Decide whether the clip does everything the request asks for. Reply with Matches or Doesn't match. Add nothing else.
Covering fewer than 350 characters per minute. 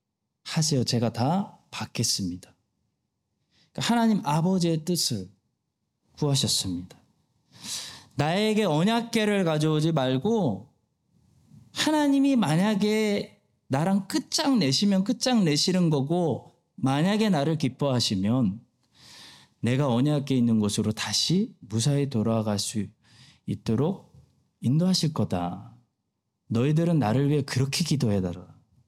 Matches